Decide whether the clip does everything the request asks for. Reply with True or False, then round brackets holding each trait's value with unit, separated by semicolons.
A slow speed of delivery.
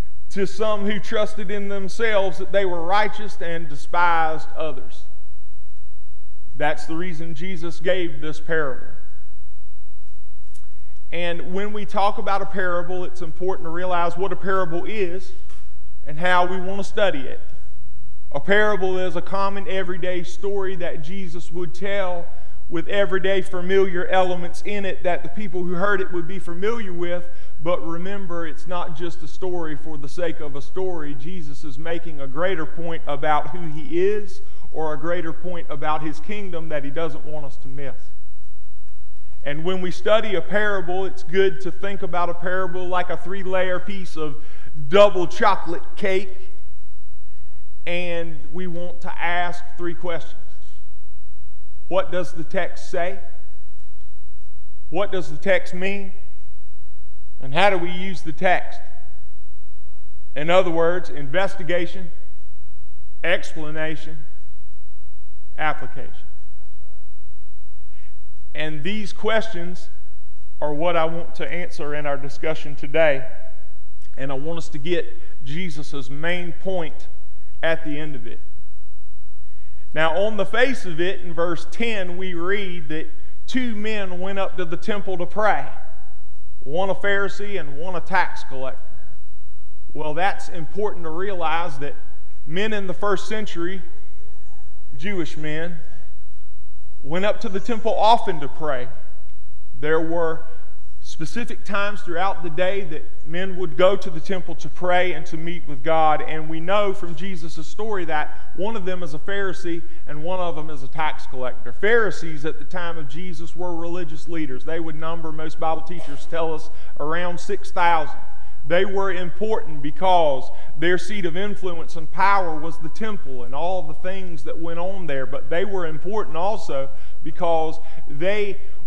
False (150 wpm)